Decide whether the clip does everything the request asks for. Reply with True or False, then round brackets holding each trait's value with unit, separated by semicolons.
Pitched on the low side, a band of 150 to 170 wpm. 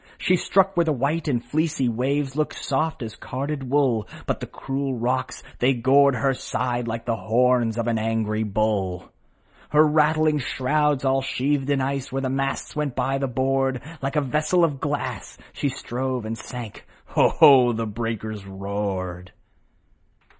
True (130 Hz; 165 wpm)